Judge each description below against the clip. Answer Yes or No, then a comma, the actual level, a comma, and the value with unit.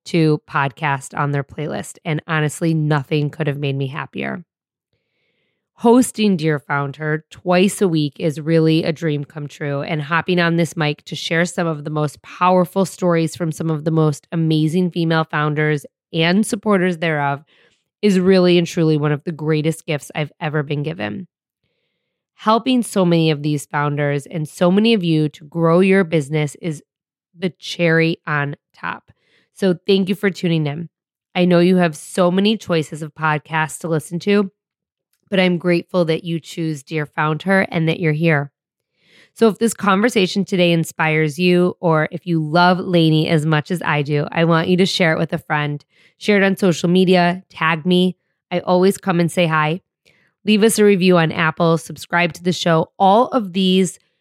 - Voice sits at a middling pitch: Yes, medium, 165 Hz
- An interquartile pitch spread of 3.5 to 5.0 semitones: No, average, 2.9 semitones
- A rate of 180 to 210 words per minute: Yes, average, 185 wpm